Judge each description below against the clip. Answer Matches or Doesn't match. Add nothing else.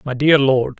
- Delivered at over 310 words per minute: Doesn't match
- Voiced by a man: Matches